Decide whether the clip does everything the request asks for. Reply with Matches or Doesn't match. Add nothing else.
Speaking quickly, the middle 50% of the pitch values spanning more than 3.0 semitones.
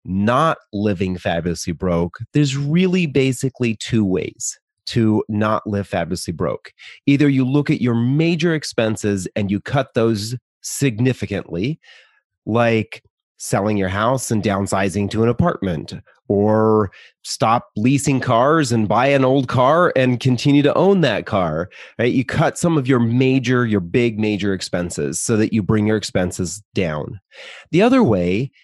Doesn't match